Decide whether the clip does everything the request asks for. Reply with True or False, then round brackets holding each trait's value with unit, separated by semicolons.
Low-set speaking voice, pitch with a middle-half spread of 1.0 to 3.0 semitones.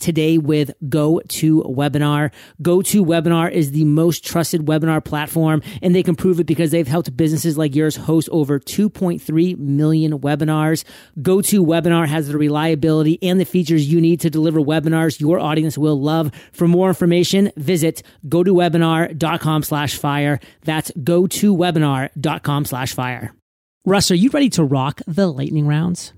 False (160 Hz; 2.4 semitones)